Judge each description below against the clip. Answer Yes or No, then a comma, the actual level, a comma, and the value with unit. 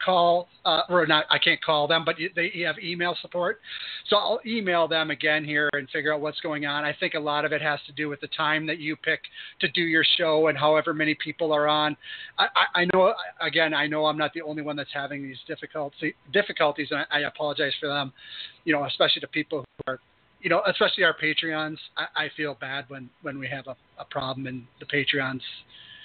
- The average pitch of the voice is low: No, medium, 150 Hz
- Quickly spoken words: Yes, fast, 230 wpm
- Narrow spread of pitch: Yes, narrow, 2.1 semitones